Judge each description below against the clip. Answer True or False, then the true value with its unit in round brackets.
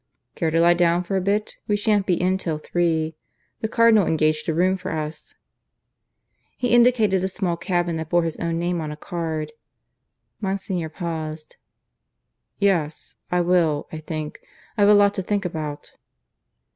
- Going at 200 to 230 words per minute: False (165 wpm)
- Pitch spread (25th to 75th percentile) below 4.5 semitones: True (3.3 semitones)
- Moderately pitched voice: True (175 Hz)